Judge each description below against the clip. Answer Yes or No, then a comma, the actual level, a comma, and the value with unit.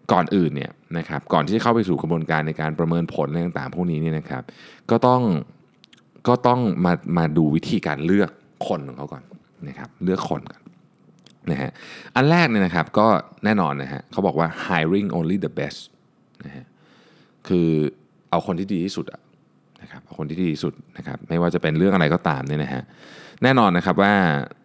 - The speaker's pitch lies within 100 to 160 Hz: No, very low, 85 Hz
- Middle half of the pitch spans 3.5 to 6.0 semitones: No, average, 3.0 semitones